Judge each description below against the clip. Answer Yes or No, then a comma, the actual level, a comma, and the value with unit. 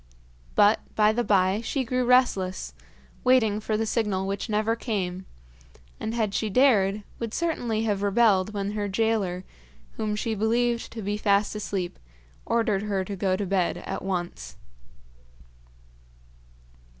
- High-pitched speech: Yes, high, 210 Hz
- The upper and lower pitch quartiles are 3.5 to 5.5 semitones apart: No, narrow, 2.6 semitones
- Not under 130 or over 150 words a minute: Yes, average, 140 wpm